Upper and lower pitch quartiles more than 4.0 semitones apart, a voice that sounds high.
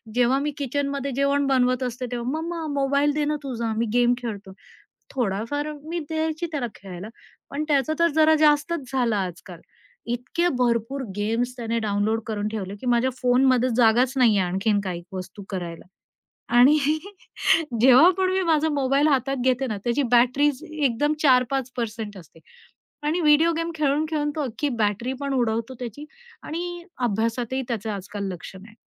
Yes: average, 4.6 semitones; very high, 255 Hz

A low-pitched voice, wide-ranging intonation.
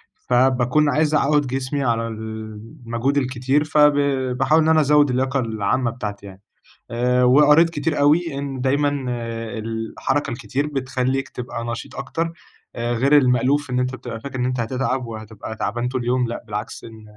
No: low, 130 Hz; average, 3.5 semitones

